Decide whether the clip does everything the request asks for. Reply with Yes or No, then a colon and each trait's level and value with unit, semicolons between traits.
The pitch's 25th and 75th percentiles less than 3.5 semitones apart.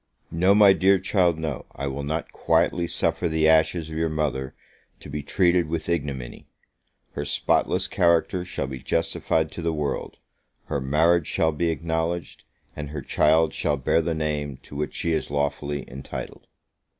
Yes: average, 2.7 semitones